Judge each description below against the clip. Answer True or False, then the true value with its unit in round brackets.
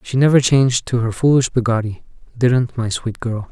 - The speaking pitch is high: False (120 Hz)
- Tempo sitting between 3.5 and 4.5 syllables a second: False (5.2 syllables/s)